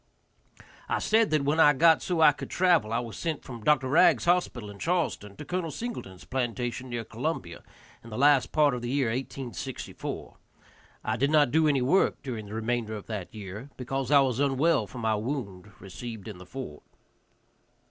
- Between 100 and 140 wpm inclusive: No, average, 190 wpm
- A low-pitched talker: Yes, low, 130 Hz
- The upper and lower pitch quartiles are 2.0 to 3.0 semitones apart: No, average, 5.1 semitones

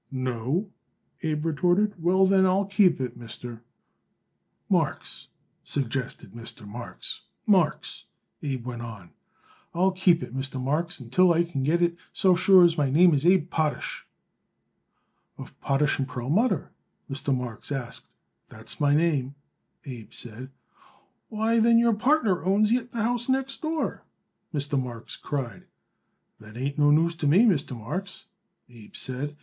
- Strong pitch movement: Yes, wide, 6.6 semitones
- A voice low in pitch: No, medium, 150 Hz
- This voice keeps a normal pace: Yes, average, 145 wpm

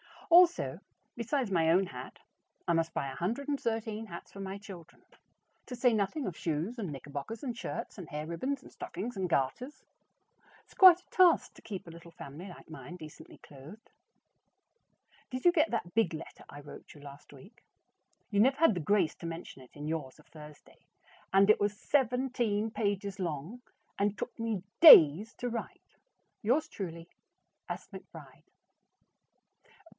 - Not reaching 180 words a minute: Yes, average, 160 wpm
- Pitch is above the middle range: Yes, high, 200 Hz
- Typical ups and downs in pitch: No, wide, 6.6 semitones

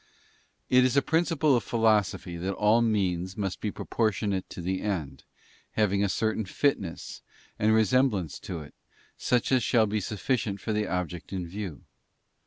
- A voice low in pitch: Yes, low, 105 Hz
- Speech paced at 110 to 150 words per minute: No, average, 165 wpm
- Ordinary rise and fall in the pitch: Yes, average, 3.5 semitones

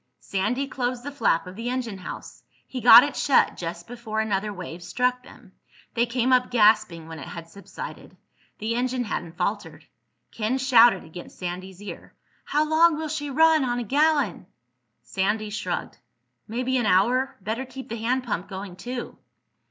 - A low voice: No, high, 235 Hz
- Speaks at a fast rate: No, average, 165 wpm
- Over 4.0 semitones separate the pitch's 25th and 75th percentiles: Yes, average, 5.0 semitones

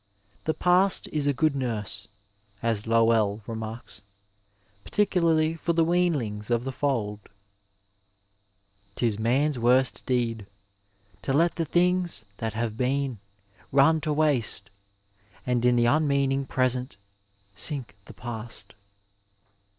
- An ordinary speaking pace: No, slow, 115 wpm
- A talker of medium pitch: No, low, 130 Hz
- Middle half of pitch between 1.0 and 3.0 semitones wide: No, average, 5.3 semitones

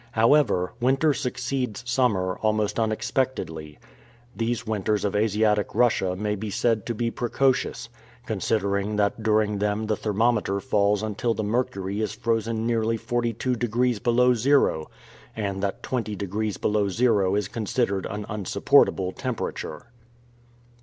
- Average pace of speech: No, slow, 130 wpm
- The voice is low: Yes, low, 110 Hz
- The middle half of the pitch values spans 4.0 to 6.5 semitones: No, average, 2.8 semitones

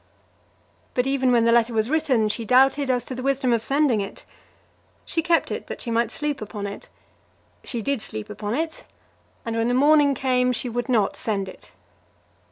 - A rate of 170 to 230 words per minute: Yes, average, 190 wpm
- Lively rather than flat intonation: No, average, 3.3 semitones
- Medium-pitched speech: No, very high, 250 Hz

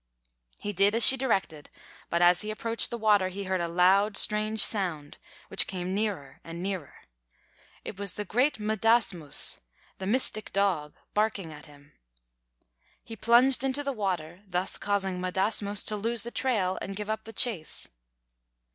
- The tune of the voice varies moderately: Yes, average, 3.4 semitones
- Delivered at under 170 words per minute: Yes, average, 160 wpm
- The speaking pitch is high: Yes, high, 200 Hz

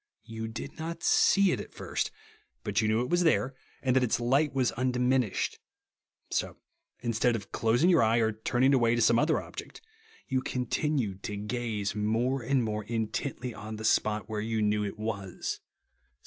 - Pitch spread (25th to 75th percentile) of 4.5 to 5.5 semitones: No, average, 3.3 semitones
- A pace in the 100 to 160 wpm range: No, average, 180 wpm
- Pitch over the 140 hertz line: No, low, 115 Hz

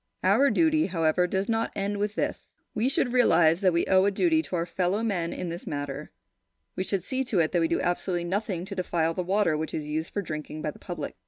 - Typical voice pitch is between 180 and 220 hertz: Yes, medium, 185 Hz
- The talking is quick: Yes, fast, 235 wpm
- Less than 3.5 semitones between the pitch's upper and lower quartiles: No, average, 3.9 semitones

